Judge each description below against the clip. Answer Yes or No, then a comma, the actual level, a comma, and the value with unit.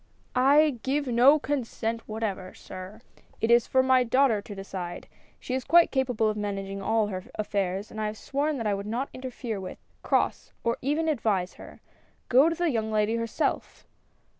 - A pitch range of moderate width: Yes, average, 4.2 semitones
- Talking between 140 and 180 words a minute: No, average, 190 wpm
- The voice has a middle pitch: No, high, 230 Hz